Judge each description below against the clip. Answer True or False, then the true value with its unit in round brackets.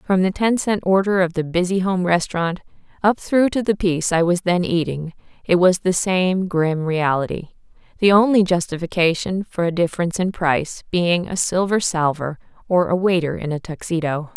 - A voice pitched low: False (175 Hz)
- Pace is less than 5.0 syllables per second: False (5.1 syllables/s)